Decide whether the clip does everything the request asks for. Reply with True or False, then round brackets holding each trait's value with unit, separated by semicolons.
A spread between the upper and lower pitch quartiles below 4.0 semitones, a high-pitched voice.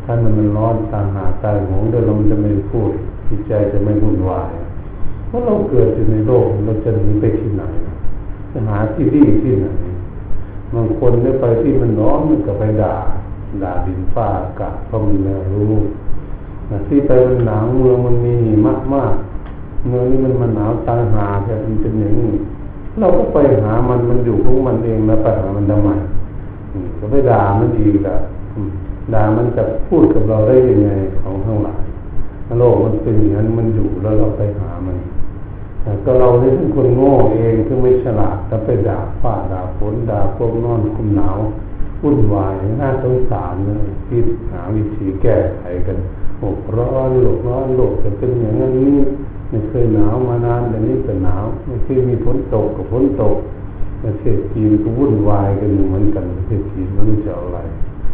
False (2.8 semitones; 105 Hz)